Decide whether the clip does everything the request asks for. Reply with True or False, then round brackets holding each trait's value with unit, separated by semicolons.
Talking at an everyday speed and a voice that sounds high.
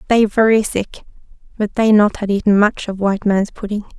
True (195 wpm; 210 Hz)